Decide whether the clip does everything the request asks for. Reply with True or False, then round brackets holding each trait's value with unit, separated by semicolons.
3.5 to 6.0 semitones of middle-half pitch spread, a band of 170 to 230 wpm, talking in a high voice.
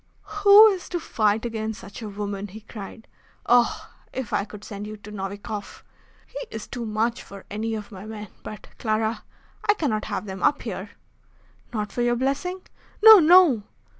True (3.9 semitones; 175 wpm; 220 Hz)